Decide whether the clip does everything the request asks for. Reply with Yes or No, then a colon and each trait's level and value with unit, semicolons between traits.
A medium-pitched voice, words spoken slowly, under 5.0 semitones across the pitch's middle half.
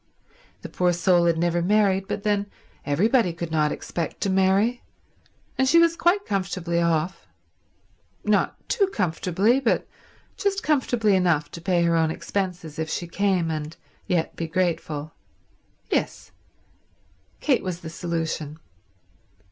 Yes: medium, 180 Hz; slow, 130 wpm; average, 3.8 semitones